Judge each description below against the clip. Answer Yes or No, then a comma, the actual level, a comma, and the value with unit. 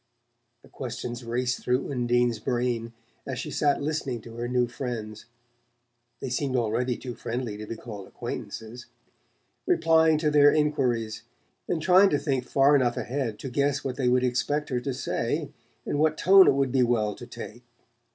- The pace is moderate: Yes, average, 170 wpm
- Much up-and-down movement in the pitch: No, average, 3.2 semitones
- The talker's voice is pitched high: No, low, 125 Hz